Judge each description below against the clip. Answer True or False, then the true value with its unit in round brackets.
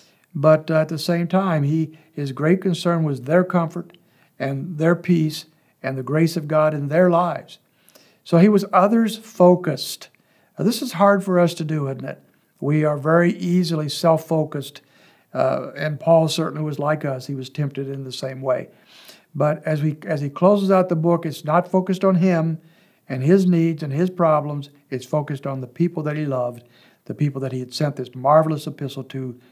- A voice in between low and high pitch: True (155 Hz)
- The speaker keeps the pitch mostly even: False (3.3 semitones)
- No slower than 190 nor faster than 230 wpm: True (195 wpm)